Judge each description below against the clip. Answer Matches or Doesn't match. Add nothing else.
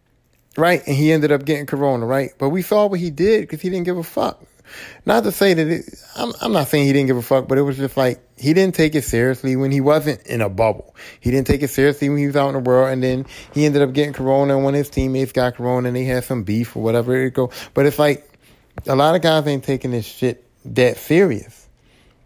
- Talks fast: Matches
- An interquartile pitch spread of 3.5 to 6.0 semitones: Doesn't match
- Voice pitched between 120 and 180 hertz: Matches